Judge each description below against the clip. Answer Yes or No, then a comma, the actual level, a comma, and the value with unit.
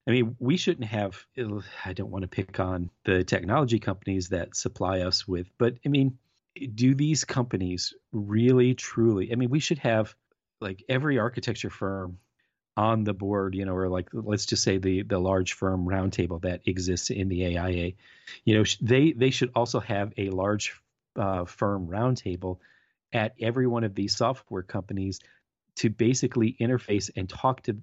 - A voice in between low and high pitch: No, low, 105 Hz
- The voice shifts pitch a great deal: No, average, 4.4 semitones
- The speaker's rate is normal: Yes, average, 170 wpm